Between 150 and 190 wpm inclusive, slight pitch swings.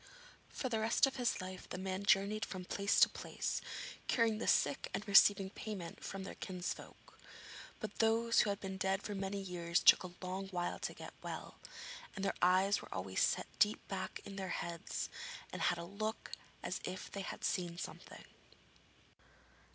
Yes: average, 180 wpm; narrow, 2.1 semitones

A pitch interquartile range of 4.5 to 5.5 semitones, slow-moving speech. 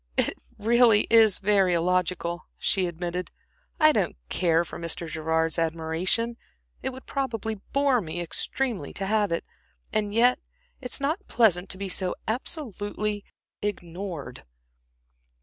Yes: average, 5.0 semitones; slow, 130 wpm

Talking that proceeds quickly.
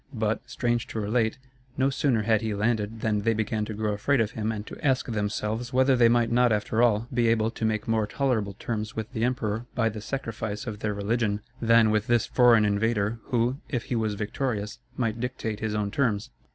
Yes: fast, 210 wpm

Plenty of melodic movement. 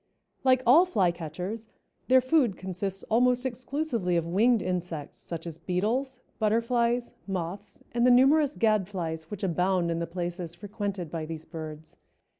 Yes: wide, 6.0 semitones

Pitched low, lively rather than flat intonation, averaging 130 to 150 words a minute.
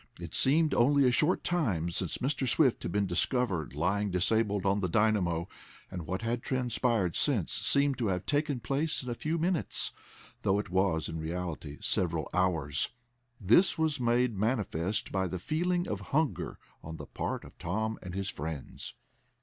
No: low, 105 Hz; wide, 6.7 semitones; average, 170 wpm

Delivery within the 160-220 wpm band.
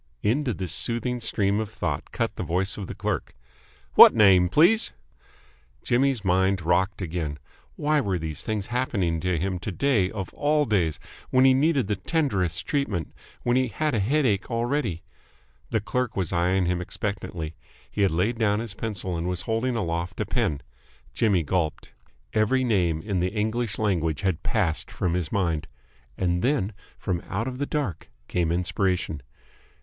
Yes: average, 165 wpm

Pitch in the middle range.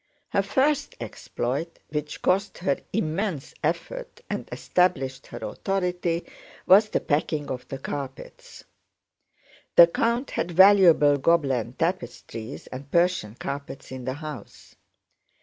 Yes: medium, 165 Hz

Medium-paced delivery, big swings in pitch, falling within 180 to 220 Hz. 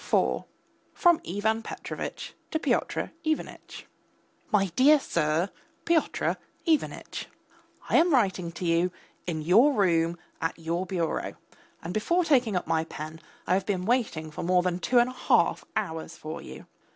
Yes: average, 150 wpm; wide, 6.8 semitones; medium, 185 Hz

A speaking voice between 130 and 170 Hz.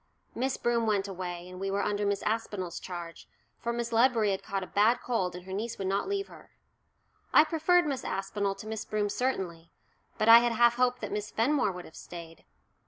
No: high, 210 Hz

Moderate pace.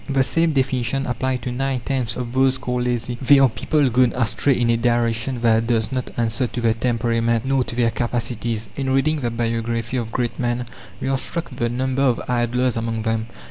No: fast, 210 wpm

